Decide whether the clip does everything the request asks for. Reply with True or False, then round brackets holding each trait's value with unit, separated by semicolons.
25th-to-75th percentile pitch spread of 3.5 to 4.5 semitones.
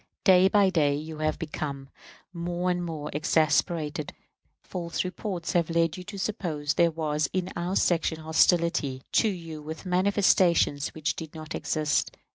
False (2.7 semitones)